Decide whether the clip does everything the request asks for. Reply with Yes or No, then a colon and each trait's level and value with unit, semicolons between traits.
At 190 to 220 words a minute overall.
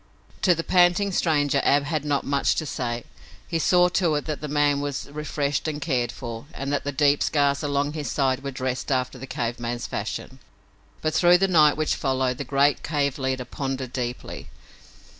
Yes: average, 195 wpm